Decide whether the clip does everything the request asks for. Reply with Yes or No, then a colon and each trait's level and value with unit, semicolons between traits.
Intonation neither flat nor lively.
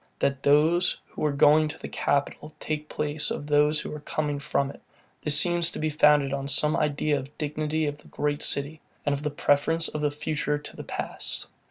No: narrow, 1.0 semitones